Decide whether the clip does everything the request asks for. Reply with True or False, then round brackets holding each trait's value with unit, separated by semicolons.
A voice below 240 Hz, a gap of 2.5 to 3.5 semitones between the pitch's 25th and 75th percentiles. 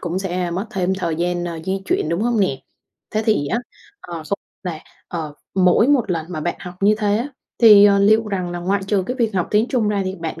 True (190 Hz; 3.2 semitones)